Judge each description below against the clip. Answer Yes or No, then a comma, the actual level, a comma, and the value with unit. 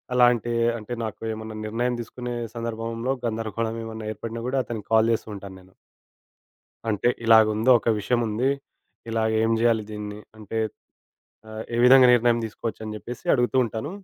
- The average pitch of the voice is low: Yes, low, 115 Hz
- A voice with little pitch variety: Yes, narrow, 1.7 semitones